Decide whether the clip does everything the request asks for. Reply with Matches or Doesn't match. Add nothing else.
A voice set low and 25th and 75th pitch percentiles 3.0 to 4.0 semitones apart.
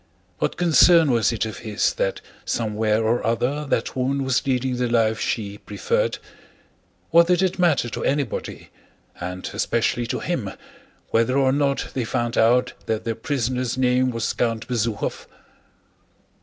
Matches